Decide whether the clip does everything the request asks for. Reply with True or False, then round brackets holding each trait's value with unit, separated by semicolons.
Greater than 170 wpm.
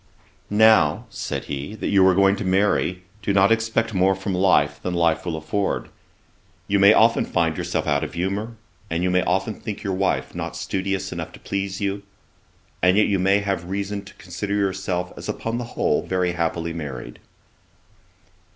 True (180 wpm)